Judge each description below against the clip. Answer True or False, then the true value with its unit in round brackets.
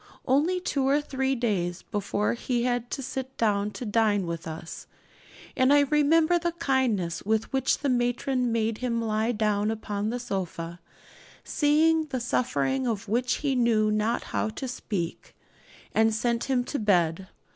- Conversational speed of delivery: True (165 wpm)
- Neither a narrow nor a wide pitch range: True (4.1 semitones)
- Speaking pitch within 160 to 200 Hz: False (235 Hz)